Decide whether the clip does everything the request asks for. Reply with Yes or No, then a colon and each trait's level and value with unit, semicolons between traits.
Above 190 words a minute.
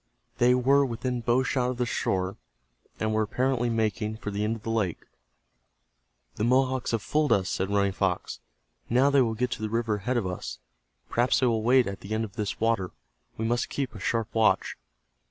Yes: fast, 205 wpm